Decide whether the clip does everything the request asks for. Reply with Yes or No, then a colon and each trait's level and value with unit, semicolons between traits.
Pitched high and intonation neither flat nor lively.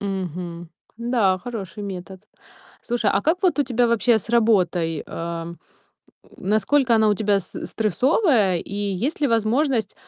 Yes: high, 210 Hz; average, 4.4 semitones